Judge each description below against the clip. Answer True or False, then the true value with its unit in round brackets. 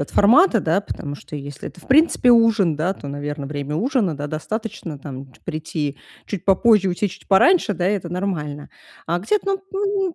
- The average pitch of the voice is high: False (180 Hz)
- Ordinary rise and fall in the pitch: False (7.2 semitones)